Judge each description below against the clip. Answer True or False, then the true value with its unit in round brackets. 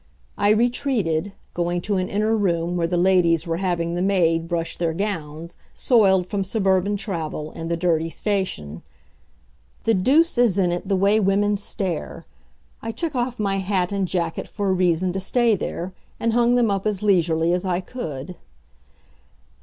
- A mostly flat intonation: False (3.4 semitones)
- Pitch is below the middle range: False (190 Hz)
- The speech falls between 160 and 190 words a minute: True (170 wpm)